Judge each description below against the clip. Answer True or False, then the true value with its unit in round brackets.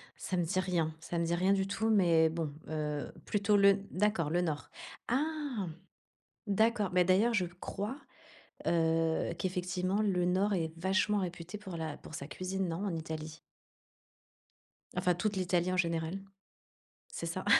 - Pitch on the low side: False (180 Hz)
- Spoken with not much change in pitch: False (3.2 semitones)